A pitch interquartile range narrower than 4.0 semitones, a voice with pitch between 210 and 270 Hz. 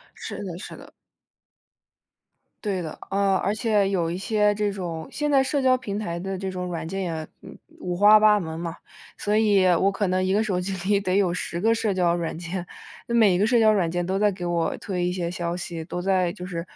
No: average, 2.9 semitones; high, 190 Hz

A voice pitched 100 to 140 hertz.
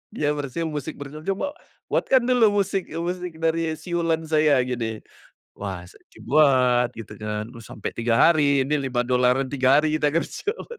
No: medium, 150 Hz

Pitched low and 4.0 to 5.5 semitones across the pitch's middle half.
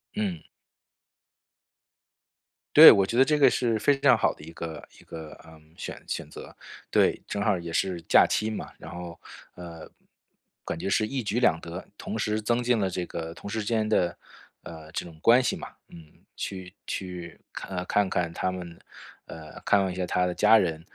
Yes: very low, 90 Hz; average, 4.3 semitones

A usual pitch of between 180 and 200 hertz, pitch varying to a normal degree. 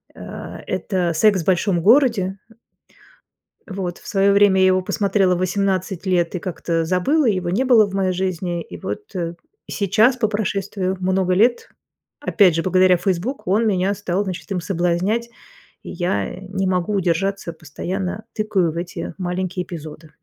No: medium, 185 Hz; narrow, 2.3 semitones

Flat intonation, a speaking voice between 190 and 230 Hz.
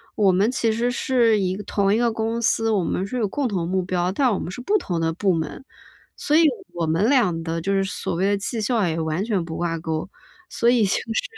No: average, 4.7 semitones; high, 200 Hz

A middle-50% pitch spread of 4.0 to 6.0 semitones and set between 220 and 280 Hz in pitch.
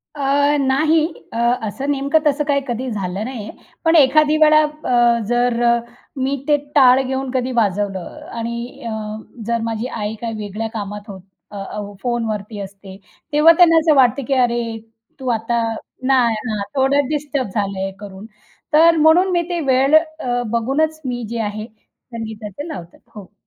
Yes: average, 4.8 semitones; very high, 250 Hz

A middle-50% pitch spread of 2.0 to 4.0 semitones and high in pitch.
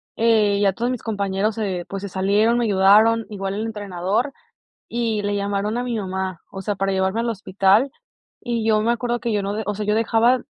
Yes: average, 2.7 semitones; high, 210 Hz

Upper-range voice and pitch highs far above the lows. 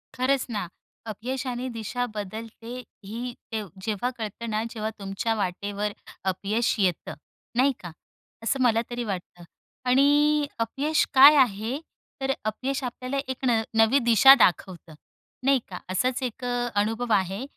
No: high, 230 Hz; average, 3.9 semitones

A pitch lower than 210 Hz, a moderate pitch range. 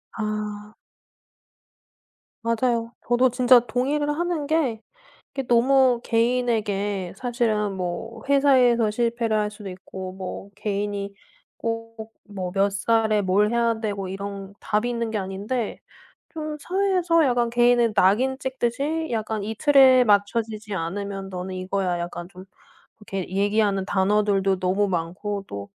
No: high, 215 Hz; average, 3.6 semitones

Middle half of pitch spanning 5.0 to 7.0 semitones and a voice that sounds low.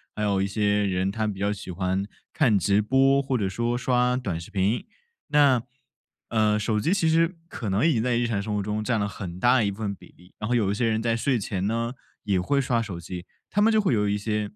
No: average, 3.7 semitones; low, 105 Hz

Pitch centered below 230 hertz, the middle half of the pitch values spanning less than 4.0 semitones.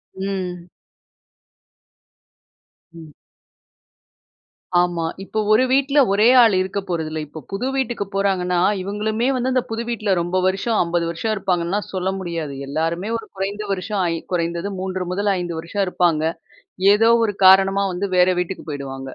Yes: high, 190 Hz; average, 3.3 semitones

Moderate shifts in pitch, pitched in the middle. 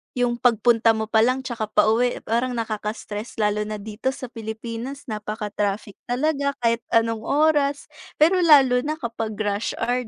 No: average, 3.0 semitones; high, 230 Hz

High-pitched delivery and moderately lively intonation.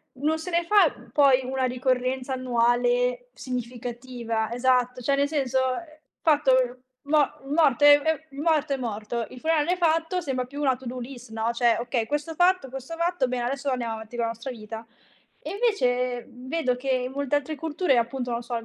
Yes: very high, 255 Hz; average, 3.2 semitones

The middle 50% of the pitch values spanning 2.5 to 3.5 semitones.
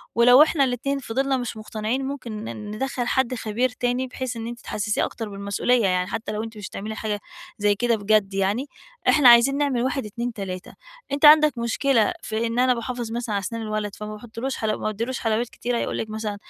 Yes: average, 2.9 semitones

